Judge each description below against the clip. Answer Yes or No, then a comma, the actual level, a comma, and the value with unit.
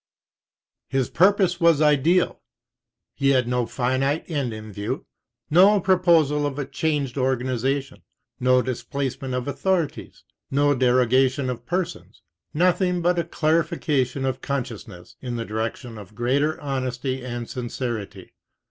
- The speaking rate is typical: No, slow, 130 wpm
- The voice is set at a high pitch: No, low, 135 Hz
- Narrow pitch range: No, average, 3.9 semitones